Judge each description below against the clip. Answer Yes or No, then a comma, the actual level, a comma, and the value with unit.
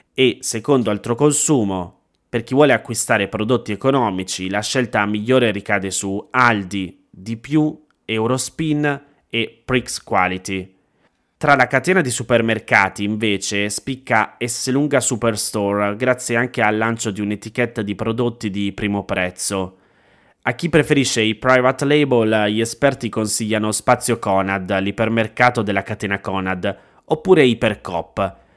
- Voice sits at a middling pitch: No, low, 110 Hz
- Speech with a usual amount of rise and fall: Yes, average, 4.0 semitones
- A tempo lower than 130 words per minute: Yes, average, 120 wpm